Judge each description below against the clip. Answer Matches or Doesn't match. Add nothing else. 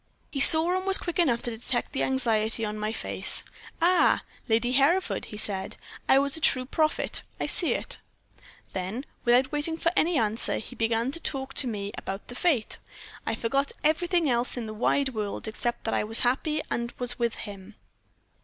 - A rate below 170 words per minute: Doesn't match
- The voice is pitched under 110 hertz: Doesn't match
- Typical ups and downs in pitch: Matches